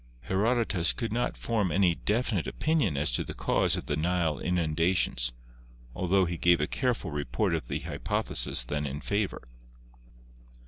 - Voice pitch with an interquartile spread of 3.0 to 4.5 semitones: No, wide, 5.6 semitones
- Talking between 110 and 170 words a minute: Yes, average, 150 wpm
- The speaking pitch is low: Yes, very low, 90 Hz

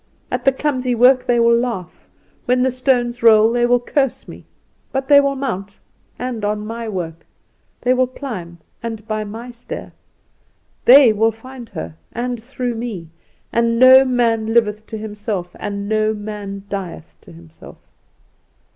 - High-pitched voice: Yes, high, 230 Hz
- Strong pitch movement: No, average, 3.1 semitones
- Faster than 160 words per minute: No, average, 155 wpm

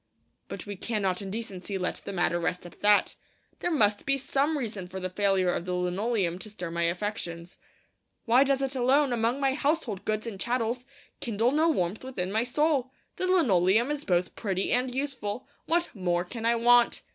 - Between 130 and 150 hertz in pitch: No, high, 220 Hz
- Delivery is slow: No, average, 190 wpm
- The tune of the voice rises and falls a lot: Yes, wide, 5.9 semitones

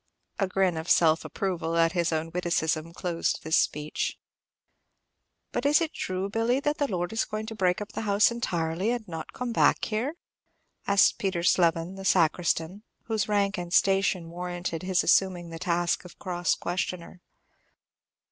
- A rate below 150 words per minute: No, average, 155 wpm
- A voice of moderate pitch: Yes, medium, 180 Hz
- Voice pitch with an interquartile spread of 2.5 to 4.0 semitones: Yes, average, 3.3 semitones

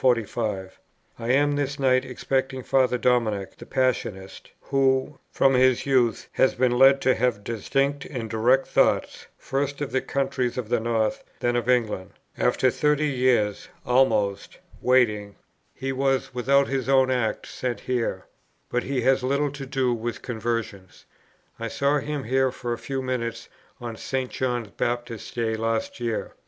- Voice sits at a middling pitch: No, low, 125 Hz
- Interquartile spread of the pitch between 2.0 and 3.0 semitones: Yes, narrow, 2.6 semitones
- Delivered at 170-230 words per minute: No, average, 155 wpm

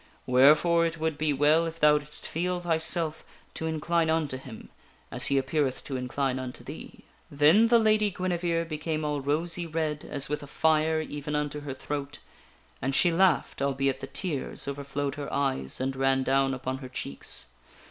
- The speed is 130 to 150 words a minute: No, average, 175 wpm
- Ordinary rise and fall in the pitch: Yes, average, 3.1 semitones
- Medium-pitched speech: Yes, medium, 150 Hz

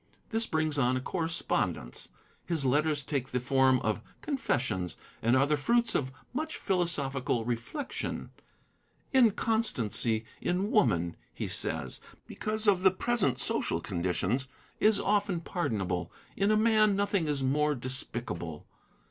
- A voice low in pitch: No, medium, 145 Hz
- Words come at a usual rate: No, slow, 130 wpm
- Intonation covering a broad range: Yes, wide, 8.7 semitones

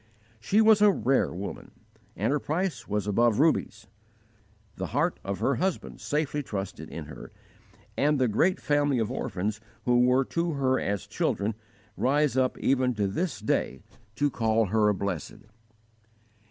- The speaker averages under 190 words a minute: Yes, average, 155 wpm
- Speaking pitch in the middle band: No, low, 125 Hz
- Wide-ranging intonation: Yes, wide, 5.8 semitones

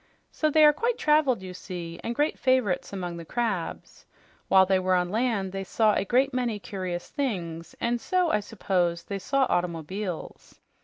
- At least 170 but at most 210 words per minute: Yes, average, 175 wpm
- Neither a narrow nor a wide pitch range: No, wide, 6.0 semitones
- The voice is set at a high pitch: Yes, high, 200 Hz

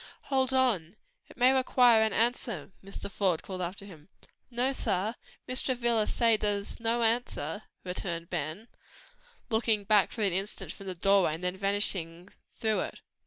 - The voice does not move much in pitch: No, average, 4.3 semitones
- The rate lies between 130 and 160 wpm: Yes, average, 155 wpm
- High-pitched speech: Yes, high, 205 Hz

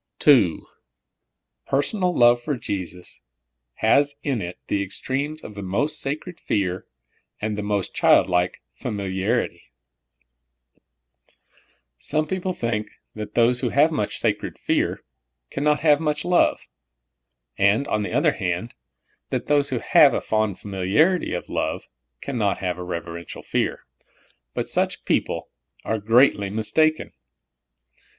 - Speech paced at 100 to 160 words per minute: Yes, slow, 135 wpm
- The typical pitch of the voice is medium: No, low, 115 Hz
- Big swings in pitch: Yes, wide, 6.6 semitones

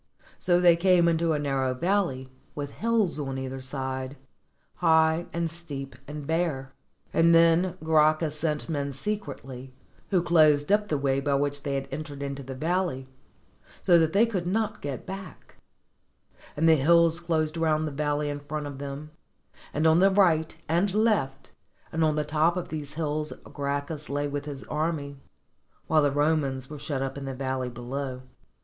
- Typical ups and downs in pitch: Yes, average, 3.3 semitones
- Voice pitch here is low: No, medium, 150 Hz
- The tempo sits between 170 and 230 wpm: Yes, average, 175 wpm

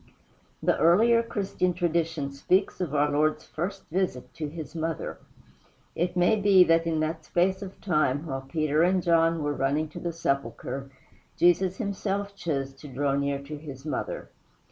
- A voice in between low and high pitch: Yes, medium, 165 Hz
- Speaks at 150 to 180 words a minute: Yes, average, 165 wpm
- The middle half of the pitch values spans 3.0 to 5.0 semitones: Yes, average, 3.8 semitones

